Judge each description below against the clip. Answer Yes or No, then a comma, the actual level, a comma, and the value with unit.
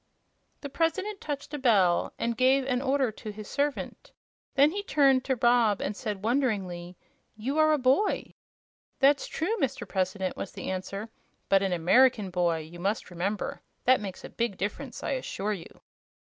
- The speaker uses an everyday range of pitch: No, wide, 6.0 semitones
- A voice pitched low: No, high, 235 Hz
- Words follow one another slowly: No, average, 170 wpm